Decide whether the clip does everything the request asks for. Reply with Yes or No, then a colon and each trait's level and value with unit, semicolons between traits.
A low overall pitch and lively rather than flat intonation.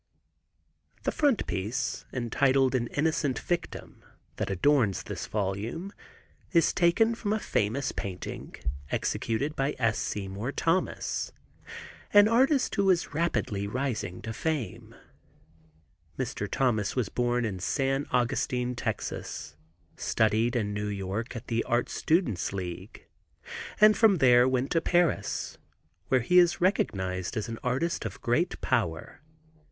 Yes: low, 125 Hz; wide, 7.5 semitones